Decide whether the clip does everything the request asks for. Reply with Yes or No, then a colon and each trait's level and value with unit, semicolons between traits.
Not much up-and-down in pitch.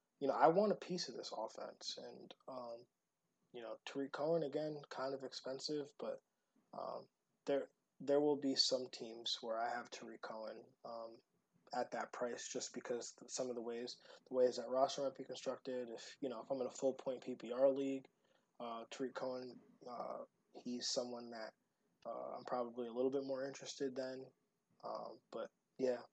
Yes: narrow, 2.0 semitones